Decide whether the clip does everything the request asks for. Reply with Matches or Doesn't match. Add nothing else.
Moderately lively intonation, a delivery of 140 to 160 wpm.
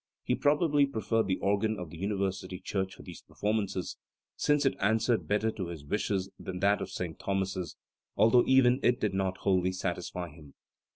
Doesn't match